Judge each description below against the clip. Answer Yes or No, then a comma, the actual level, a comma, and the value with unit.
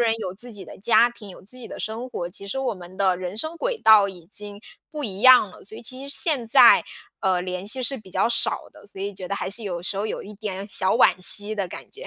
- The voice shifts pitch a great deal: No, average, 4.0 semitones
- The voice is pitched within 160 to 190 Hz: No, high, 210 Hz